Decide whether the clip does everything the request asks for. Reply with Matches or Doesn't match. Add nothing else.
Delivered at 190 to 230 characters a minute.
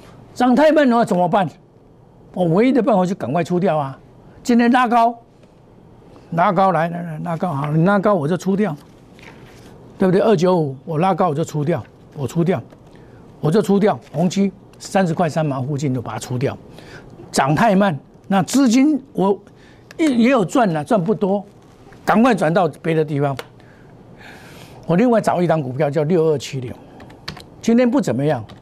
Doesn't match